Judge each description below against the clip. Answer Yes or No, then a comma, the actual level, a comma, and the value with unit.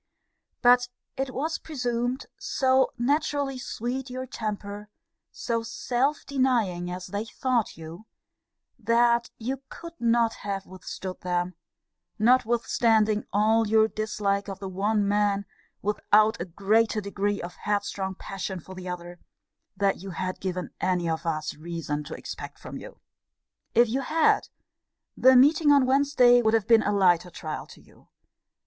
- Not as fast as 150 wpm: Yes, average, 140 wpm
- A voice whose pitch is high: Yes, high, 215 Hz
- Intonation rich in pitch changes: No, average, 4.5 semitones